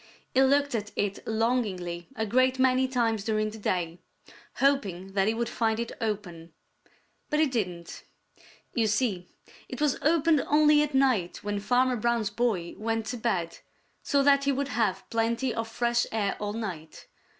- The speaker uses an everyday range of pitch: Yes, average, 4.2 semitones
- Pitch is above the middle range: Yes, high, 225 Hz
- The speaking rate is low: No, average, 165 wpm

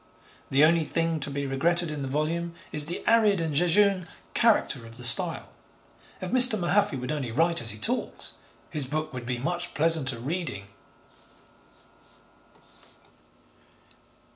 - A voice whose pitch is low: No, medium, 155 Hz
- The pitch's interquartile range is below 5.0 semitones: Yes, average, 4.5 semitones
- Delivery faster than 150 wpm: No, average, 140 wpm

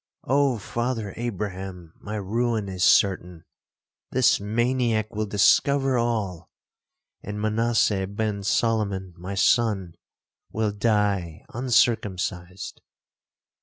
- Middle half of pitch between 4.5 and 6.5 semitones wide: No, average, 3.4 semitones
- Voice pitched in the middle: No, low, 105 Hz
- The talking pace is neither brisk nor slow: No, slow, 95 wpm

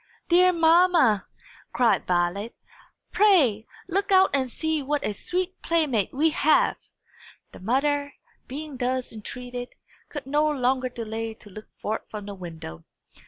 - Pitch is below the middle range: No, very high, 260 Hz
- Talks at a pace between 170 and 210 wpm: No, slow, 135 wpm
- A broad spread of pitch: Yes, wide, 6.3 semitones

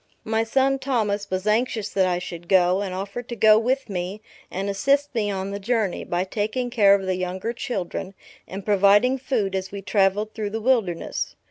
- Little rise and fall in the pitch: No, average, 3.3 semitones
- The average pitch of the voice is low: No, high, 205 Hz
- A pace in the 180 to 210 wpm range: Yes, average, 195 wpm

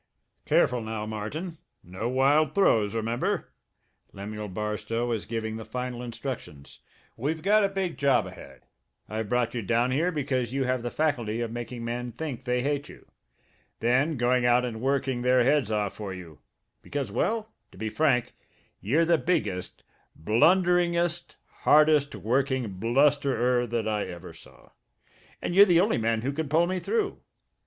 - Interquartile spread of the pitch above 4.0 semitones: Yes, average, 5.2 semitones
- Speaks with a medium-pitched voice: No, low, 125 Hz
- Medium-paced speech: Yes, average, 160 wpm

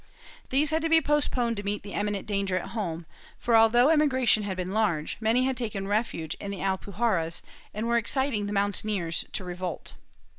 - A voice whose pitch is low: No, high, 210 Hz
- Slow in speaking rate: No, average, 190 wpm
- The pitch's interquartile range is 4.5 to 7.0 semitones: No, average, 3.8 semitones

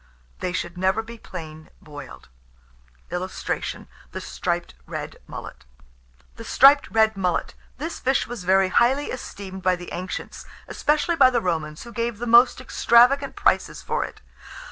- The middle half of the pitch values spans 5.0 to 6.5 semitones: Yes, wide, 5.6 semitones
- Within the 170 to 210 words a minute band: No, average, 145 wpm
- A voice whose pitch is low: No, high, 220 Hz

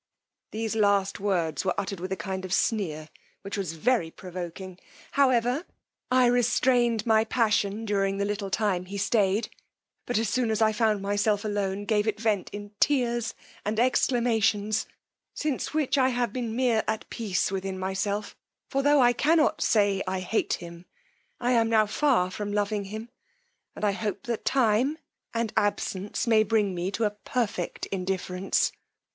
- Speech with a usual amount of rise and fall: Yes, average, 3.3 semitones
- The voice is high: Yes, high, 210 Hz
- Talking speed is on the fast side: No, average, 160 wpm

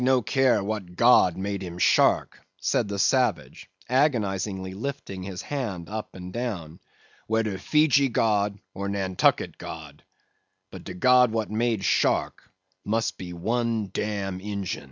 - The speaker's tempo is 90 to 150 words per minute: Yes, average, 140 wpm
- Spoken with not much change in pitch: No, average, 4.0 semitones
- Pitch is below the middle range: Yes, low, 105 Hz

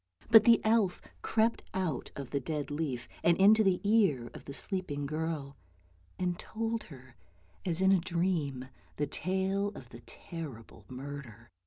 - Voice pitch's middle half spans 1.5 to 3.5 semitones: No, wide, 5.6 semitones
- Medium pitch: Yes, medium, 165 Hz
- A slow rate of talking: No, average, 155 wpm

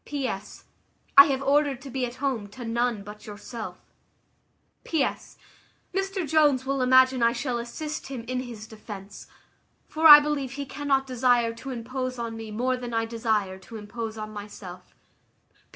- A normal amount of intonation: Yes, average, 3.3 semitones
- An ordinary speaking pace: Yes, average, 160 wpm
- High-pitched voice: Yes, high, 245 Hz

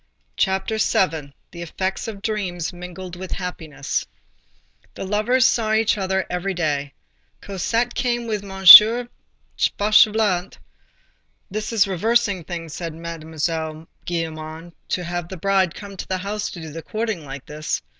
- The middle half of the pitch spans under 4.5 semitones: Yes, average, 4.1 semitones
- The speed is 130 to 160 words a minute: Yes, slow, 135 wpm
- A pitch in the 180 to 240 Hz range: Yes, medium, 185 Hz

